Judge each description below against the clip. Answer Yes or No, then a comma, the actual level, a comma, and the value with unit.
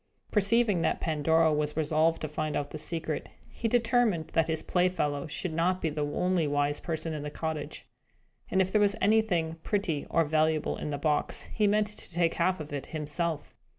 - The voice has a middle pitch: Yes, medium, 160 Hz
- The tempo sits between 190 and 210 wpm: Yes, average, 195 wpm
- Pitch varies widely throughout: No, average, 3.5 semitones